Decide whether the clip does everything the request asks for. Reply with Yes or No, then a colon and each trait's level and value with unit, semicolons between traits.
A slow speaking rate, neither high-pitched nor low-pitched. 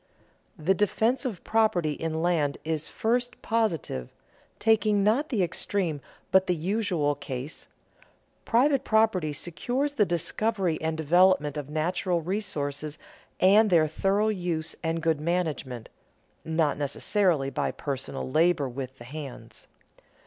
Yes: slow, 125 wpm; medium, 170 Hz